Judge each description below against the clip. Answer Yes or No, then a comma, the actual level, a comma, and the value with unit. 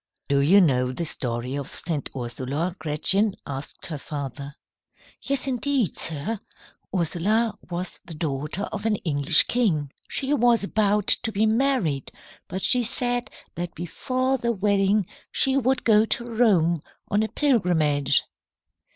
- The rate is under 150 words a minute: Yes, average, 140 wpm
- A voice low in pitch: No, high, 190 Hz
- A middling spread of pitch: No, wide, 7.5 semitones